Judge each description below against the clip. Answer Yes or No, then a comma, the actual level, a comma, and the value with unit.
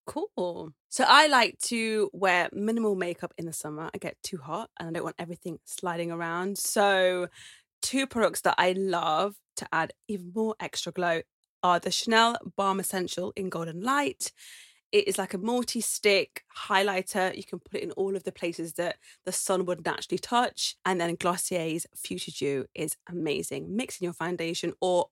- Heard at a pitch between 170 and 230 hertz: Yes, medium, 185 Hz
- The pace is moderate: Yes, average, 180 wpm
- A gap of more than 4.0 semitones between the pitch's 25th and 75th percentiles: No, average, 2.9 semitones